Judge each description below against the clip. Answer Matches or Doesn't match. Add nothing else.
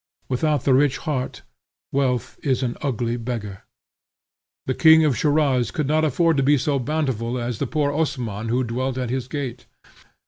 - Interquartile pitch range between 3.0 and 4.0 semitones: Matches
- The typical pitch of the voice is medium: Doesn't match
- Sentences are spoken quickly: Doesn't match